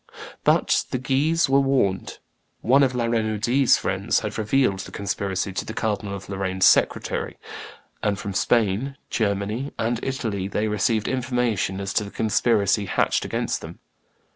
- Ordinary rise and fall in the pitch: Yes, average, 4.0 semitones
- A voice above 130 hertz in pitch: No, low, 110 Hz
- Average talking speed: Yes, average, 150 wpm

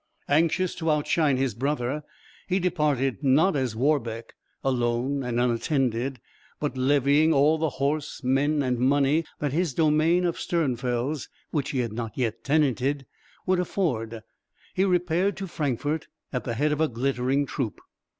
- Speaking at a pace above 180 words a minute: No, average, 150 wpm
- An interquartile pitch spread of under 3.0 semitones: No, average, 3.7 semitones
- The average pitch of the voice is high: No, medium, 140 Hz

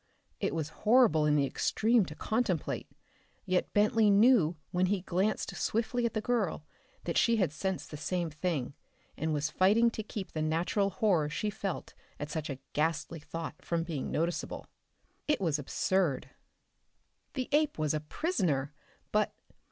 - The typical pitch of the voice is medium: Yes, medium, 180 Hz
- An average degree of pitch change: No, wide, 5.7 semitones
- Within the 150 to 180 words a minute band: Yes, average, 160 wpm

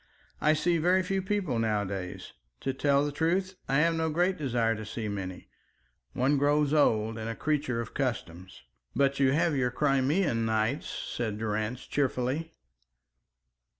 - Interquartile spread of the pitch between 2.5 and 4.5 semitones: No, wide, 5.4 semitones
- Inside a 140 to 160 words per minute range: Yes, average, 150 wpm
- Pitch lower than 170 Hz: Yes, low, 135 Hz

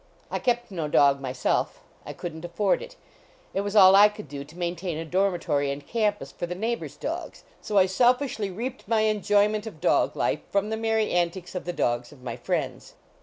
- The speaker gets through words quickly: Yes, fast, 210 wpm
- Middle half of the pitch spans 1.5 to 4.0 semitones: No, average, 4.7 semitones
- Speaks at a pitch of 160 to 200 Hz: Yes, high, 190 Hz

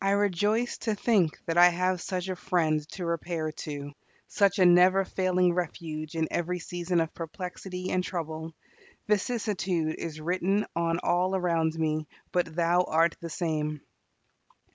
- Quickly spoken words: No, average, 150 wpm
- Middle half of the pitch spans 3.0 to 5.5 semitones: No, narrow, 2.4 semitones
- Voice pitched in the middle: Yes, medium, 175 Hz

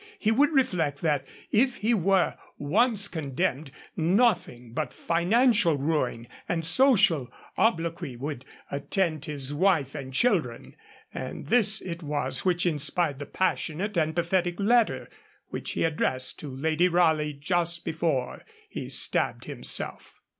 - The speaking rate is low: Yes, slow, 130 wpm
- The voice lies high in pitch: No, medium, 165 Hz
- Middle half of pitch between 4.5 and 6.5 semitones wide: Yes, average, 5.1 semitones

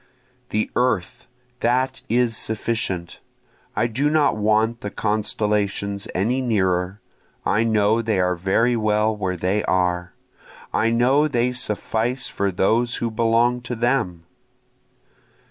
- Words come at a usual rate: No, slow, 125 wpm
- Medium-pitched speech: No, low, 110 Hz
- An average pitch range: Yes, average, 3.3 semitones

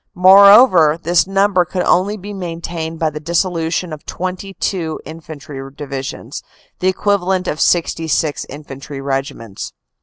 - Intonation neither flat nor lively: Yes, average, 3.6 semitones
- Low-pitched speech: No, medium, 170 Hz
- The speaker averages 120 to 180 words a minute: Yes, average, 140 wpm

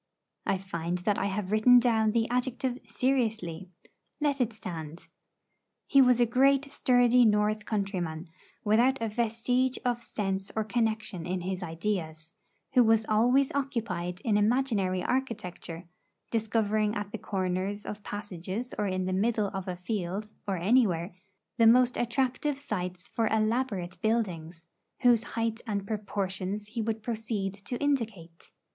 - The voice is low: No, high, 215 Hz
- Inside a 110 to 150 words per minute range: Yes, average, 140 wpm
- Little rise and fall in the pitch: No, average, 4.2 semitones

